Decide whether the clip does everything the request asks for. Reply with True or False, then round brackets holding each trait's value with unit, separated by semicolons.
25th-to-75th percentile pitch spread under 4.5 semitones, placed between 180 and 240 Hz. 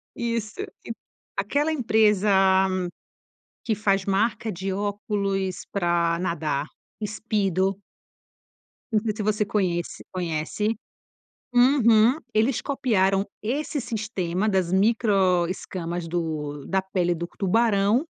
True (3.4 semitones; 200 Hz)